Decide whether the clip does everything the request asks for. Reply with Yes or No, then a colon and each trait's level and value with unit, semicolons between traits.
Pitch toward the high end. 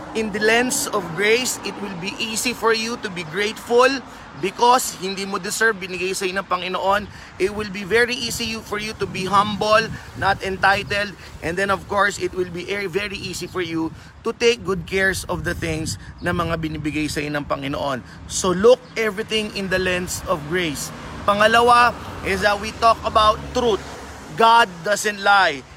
Yes: high, 200 Hz